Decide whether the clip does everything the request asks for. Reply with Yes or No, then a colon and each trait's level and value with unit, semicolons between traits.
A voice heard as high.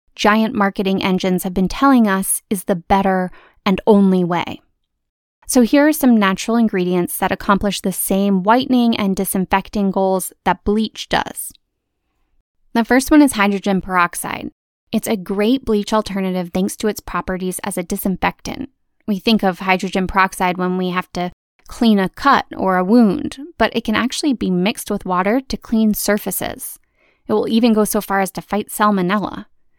Yes: high, 200 Hz